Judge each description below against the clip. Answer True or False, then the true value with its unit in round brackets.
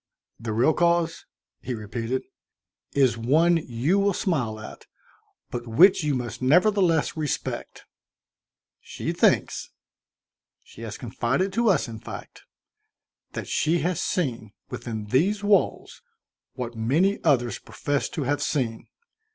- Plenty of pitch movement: True (6.7 semitones)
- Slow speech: True (130 wpm)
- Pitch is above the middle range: False (140 Hz)